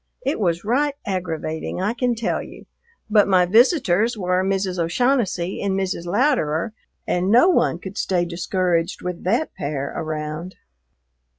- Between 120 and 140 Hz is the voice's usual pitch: No, medium, 185 Hz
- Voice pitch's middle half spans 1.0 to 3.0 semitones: No, average, 4.7 semitones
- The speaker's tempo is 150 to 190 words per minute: No, average, 140 wpm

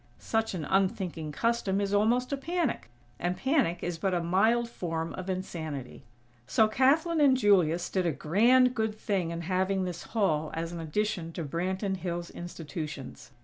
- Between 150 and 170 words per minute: Yes, average, 165 wpm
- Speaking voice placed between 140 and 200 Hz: Yes, medium, 185 Hz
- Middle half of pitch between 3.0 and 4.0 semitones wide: No, average, 4.9 semitones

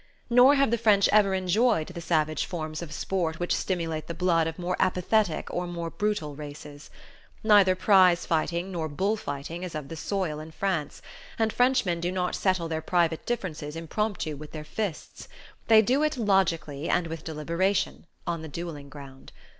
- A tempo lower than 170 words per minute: No, average, 175 wpm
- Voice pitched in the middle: Yes, medium, 175 Hz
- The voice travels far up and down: No, average, 3.8 semitones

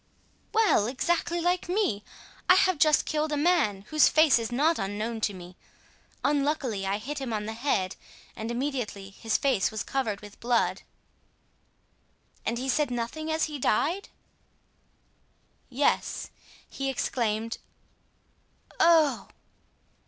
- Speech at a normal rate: No, slow, 130 wpm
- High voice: Yes, very high, 265 Hz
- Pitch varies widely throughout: Yes, wide, 6.1 semitones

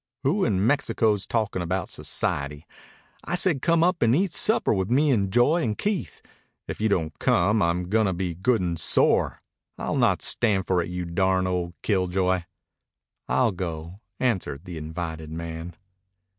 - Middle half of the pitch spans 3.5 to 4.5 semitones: No, average, 5.3 semitones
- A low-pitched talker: Yes, very low, 95 Hz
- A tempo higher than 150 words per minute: Yes, average, 165 wpm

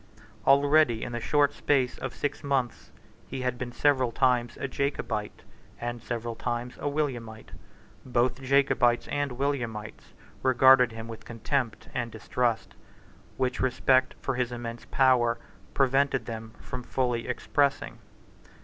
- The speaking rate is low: Yes, slow, 130 wpm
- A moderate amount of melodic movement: No, narrow, 2.3 semitones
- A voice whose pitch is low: Yes, low, 125 Hz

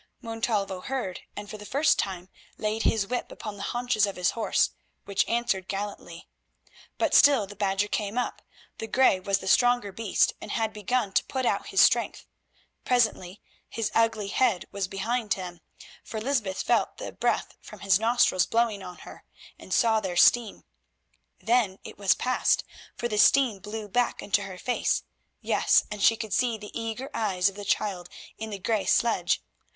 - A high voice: Yes, high, 210 Hz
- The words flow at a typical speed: Yes, average, 175 wpm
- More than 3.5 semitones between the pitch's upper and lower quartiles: No, average, 3.1 semitones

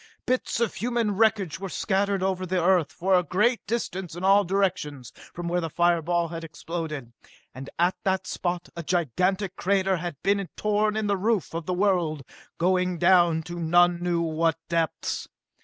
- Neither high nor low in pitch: Yes, medium, 180 Hz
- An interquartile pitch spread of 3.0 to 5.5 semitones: No, narrow, 2.5 semitones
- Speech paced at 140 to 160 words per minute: No, average, 175 wpm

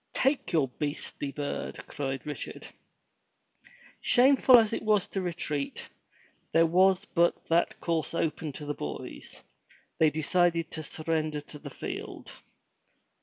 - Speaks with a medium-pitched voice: Yes, medium, 165 Hz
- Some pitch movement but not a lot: Yes, average, 3.5 semitones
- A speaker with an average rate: No, slow, 125 wpm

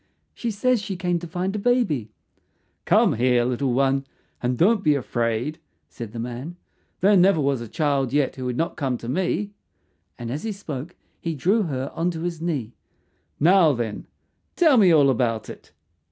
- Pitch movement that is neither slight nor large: No, wide, 6.4 semitones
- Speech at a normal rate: Yes, average, 180 wpm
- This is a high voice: No, medium, 150 Hz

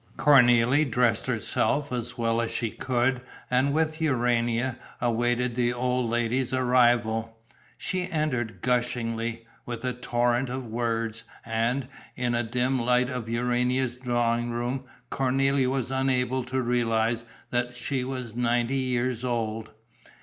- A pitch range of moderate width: No, narrow, 1.6 semitones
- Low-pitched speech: Yes, low, 120 Hz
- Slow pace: Yes, slow, 130 wpm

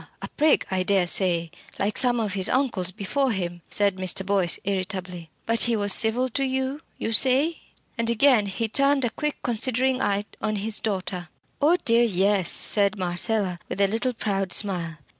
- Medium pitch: No, high, 205 Hz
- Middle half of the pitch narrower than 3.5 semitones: No, average, 4.6 semitones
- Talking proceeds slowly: No, average, 180 wpm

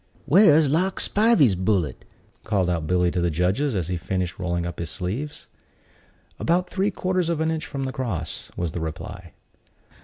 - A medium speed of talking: Yes, average, 175 wpm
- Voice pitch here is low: Yes, low, 100 Hz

